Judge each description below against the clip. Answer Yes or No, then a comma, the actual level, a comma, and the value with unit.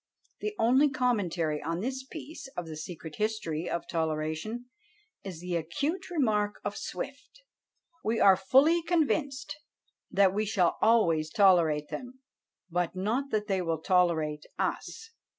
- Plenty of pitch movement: Yes, wide, 7.4 semitones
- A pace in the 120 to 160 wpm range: Yes, slow, 135 wpm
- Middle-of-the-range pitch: No, high, 200 Hz